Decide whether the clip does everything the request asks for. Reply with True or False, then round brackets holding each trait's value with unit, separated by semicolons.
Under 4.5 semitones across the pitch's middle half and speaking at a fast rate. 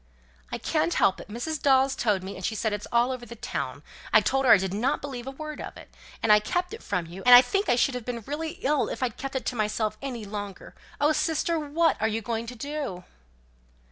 False (5.0 semitones; 250 wpm)